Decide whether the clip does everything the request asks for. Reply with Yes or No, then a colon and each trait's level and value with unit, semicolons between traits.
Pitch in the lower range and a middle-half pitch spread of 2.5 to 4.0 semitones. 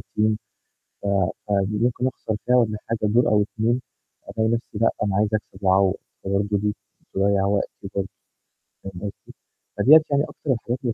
Yes: low, 105 Hz; average, 2.9 semitones